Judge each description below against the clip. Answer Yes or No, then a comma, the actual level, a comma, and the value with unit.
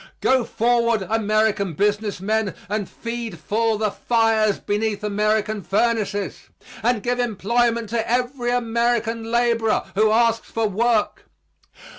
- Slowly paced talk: Yes, slow, 120 wpm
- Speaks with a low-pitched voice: No, high, 225 Hz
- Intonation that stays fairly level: Yes, narrow, 2.0 semitones